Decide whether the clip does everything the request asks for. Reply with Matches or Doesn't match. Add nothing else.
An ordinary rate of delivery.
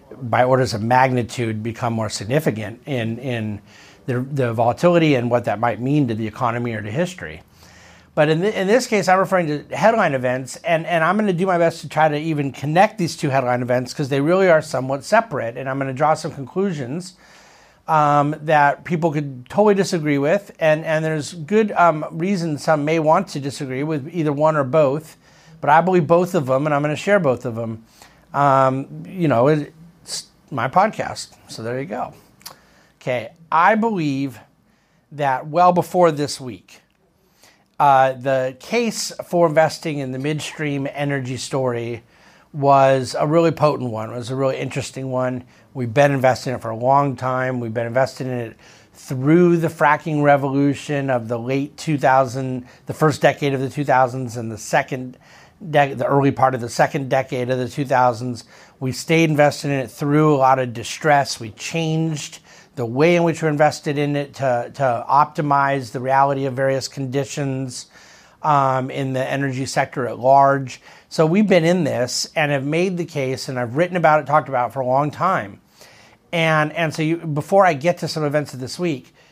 Matches